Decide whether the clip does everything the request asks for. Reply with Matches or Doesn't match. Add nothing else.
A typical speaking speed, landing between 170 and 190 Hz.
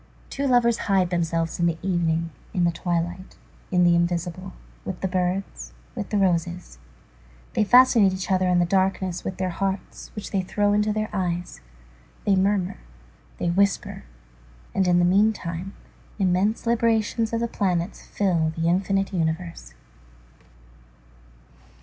Matches